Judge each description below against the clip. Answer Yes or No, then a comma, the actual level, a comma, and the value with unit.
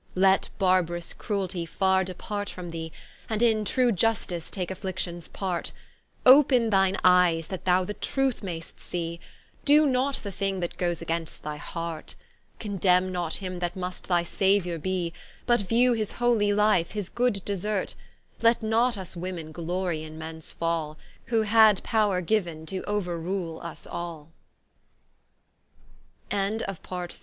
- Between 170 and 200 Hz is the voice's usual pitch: Yes, medium, 185 Hz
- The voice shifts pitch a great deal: No, average, 3.6 semitones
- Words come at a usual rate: No, slow, 130 wpm